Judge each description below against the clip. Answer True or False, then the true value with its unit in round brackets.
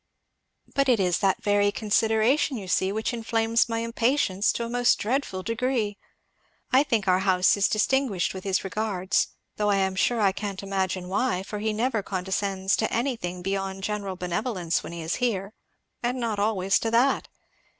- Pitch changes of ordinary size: True (3.3 semitones)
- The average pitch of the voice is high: True (205 Hz)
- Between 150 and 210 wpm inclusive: True (175 wpm)